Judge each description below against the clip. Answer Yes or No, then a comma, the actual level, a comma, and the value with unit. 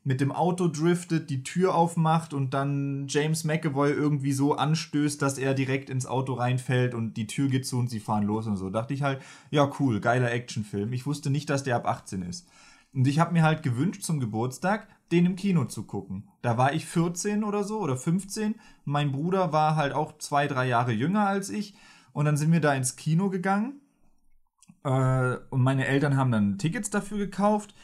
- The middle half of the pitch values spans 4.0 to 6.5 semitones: Yes, average, 4.7 semitones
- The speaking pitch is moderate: Yes, medium, 145 Hz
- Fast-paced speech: Yes, fast, 205 wpm